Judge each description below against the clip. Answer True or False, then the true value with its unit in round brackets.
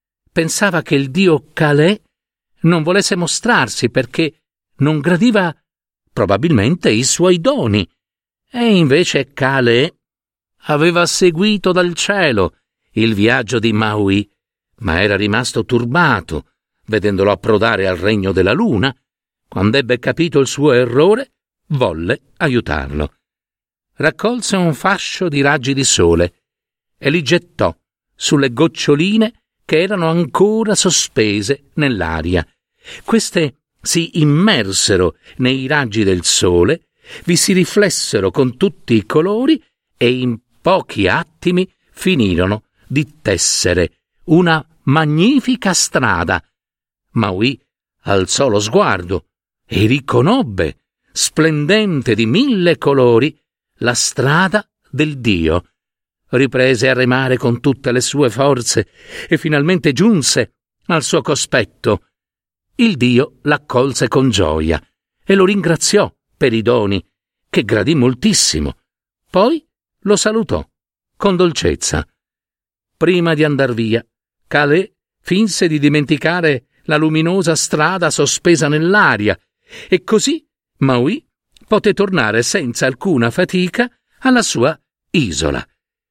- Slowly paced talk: True (110 wpm)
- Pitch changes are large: True (7.3 semitones)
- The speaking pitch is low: False (150 Hz)